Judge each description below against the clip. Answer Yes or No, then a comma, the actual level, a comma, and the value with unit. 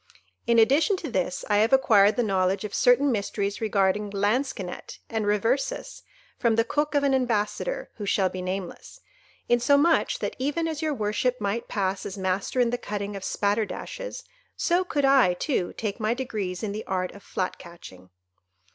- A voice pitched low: No, high, 220 Hz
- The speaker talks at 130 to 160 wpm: No, average, 170 wpm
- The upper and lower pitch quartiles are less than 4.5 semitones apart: No, average, 5.3 semitones